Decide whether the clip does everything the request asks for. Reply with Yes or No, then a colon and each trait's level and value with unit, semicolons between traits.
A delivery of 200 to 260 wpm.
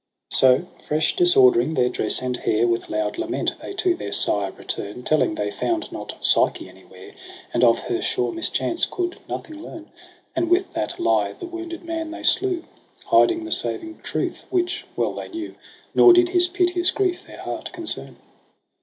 No: average, 175 wpm